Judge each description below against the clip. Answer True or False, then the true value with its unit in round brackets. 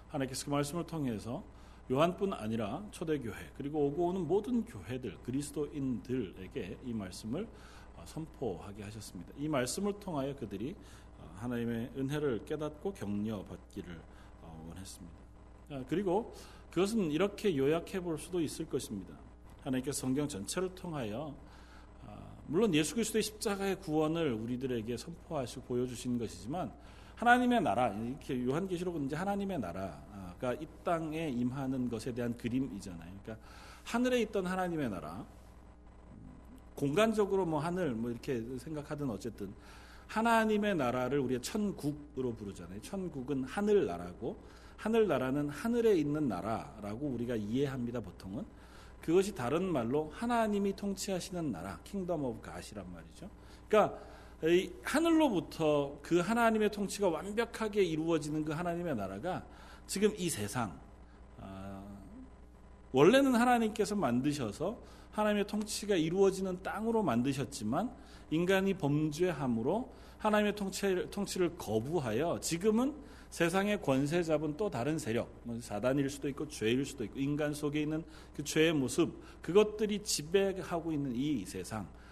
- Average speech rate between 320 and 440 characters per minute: True (330 characters per minute)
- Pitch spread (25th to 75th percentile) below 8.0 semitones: False (8.3 semitones)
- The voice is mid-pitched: True (150 Hz)